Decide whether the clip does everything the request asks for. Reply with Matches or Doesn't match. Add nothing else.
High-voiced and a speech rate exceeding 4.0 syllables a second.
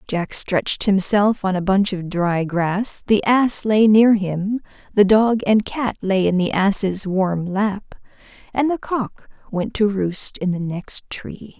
Doesn't match